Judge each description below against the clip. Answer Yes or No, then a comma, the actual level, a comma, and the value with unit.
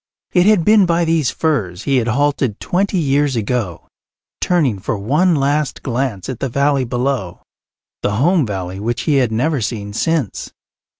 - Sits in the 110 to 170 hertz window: Yes, low, 135 Hz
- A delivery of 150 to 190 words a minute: Yes, average, 165 wpm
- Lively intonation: Yes, wide, 6.1 semitones